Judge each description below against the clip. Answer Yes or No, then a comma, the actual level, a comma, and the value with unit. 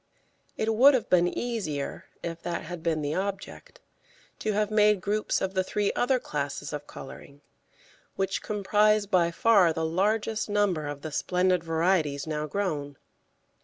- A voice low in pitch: No, medium, 185 Hz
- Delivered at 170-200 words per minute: No, average, 155 wpm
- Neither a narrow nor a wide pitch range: Yes, average, 4.9 semitones